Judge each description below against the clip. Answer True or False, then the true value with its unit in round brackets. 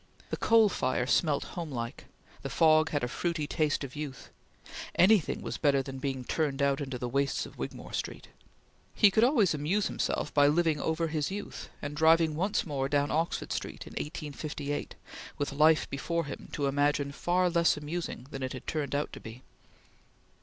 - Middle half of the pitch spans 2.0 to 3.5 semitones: True (3.0 semitones)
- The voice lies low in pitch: False (150 Hz)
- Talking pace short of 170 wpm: False (180 wpm)